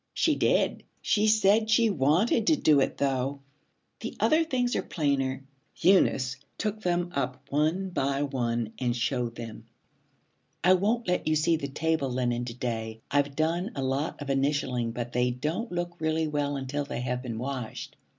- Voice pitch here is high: No, medium, 140 Hz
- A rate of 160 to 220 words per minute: Yes, average, 170 wpm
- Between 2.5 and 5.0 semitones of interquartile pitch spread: No, wide, 5.6 semitones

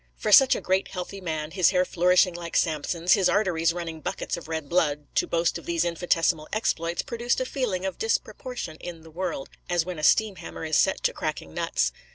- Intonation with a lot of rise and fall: No, average, 2.8 semitones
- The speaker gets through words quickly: Yes, fast, 210 wpm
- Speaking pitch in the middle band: Yes, medium, 175 Hz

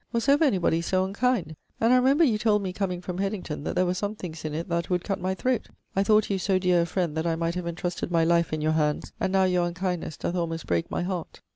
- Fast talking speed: Yes, fast, 275 wpm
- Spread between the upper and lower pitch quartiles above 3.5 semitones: No, average, 2.8 semitones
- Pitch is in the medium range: Yes, medium, 180 Hz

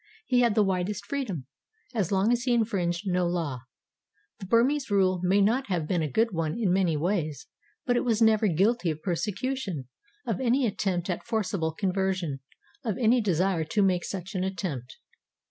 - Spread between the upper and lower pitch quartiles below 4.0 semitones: No, average, 4.4 semitones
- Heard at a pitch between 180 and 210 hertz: Yes, high, 190 Hz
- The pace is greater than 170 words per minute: Yes, average, 180 wpm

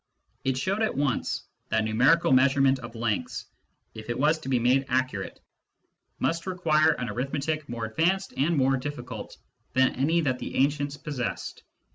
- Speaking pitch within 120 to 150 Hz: Yes, low, 135 Hz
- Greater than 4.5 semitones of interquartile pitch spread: No, average, 3.6 semitones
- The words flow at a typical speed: Yes, average, 155 wpm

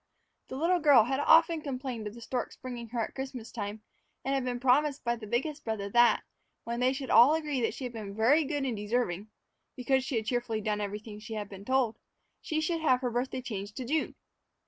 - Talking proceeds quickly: Yes, fast, 215 wpm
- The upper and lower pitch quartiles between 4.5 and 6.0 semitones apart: No, average, 3.5 semitones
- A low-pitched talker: No, high, 245 Hz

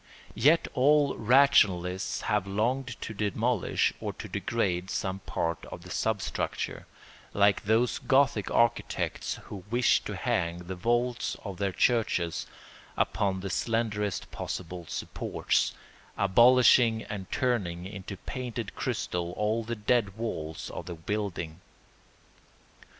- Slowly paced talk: Yes, slow, 120 wpm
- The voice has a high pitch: No, low, 105 Hz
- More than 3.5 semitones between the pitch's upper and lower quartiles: Yes, average, 4.2 semitones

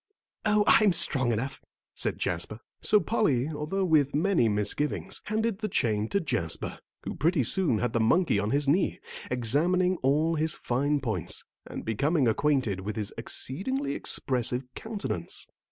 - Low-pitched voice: No, medium, 145 Hz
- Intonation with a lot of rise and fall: Yes, wide, 7.7 semitones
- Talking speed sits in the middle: Yes, average, 150 wpm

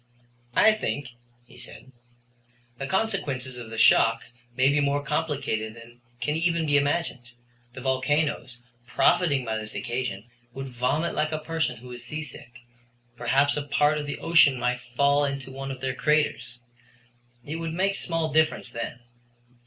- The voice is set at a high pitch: No, medium, 140 Hz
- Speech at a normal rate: Yes, average, 155 wpm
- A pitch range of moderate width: Yes, average, 3.7 semitones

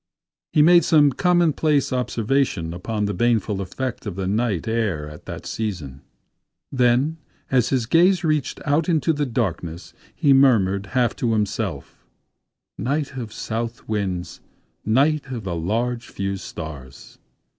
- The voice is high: No, low, 115 Hz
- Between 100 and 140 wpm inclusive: Yes, slow, 135 wpm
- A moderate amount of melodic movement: No, wide, 6.1 semitones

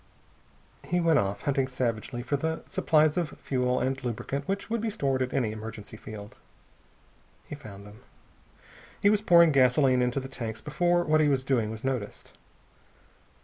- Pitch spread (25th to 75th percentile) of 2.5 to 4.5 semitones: No, average, 4.9 semitones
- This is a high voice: No, low, 135 Hz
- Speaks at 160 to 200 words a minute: Yes, average, 165 wpm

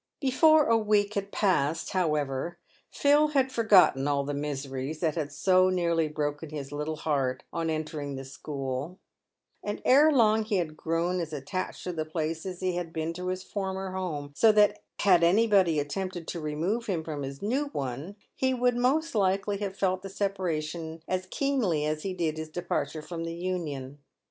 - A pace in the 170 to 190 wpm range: Yes, average, 180 wpm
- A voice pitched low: No, medium, 175 Hz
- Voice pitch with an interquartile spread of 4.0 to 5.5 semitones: Yes, average, 4.7 semitones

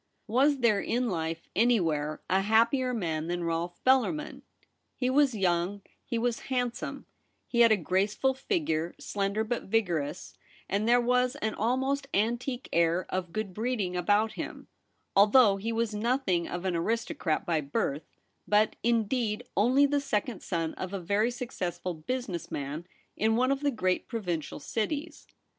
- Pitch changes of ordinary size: No, wide, 5.7 semitones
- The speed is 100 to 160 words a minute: Yes, average, 150 wpm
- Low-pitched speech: No, high, 215 Hz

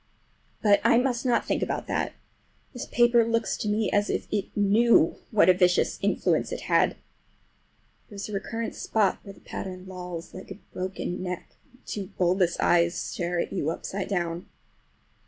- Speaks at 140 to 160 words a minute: No, average, 175 wpm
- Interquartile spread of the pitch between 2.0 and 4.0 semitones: Yes, average, 3.5 semitones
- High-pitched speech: Yes, high, 195 Hz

